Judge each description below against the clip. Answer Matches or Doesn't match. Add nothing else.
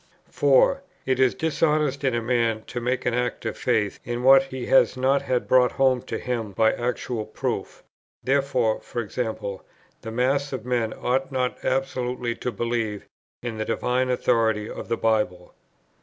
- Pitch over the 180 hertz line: Doesn't match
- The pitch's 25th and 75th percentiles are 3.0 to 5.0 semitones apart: Doesn't match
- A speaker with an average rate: Matches